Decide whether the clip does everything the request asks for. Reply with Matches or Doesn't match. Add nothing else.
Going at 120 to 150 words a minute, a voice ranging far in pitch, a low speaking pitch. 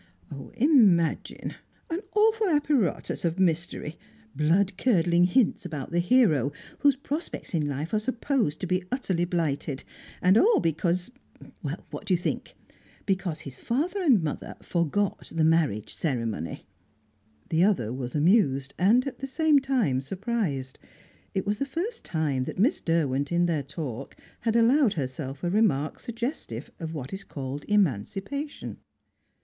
Doesn't match